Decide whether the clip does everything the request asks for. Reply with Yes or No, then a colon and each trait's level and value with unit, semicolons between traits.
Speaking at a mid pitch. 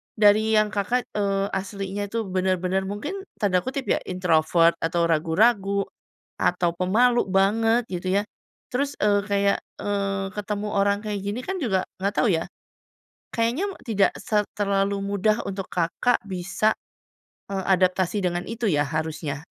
No: high, 200 Hz